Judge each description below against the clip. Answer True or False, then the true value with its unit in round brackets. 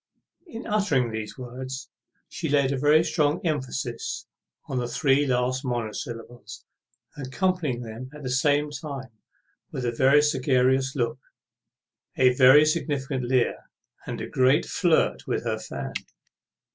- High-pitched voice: False (130 Hz)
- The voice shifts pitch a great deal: False (2.8 semitones)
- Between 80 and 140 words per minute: True (135 wpm)